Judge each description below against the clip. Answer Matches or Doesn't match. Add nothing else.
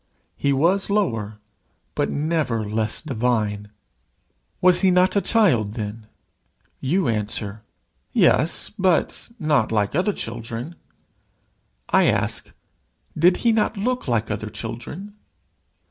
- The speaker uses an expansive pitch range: Matches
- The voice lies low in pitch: Matches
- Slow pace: Matches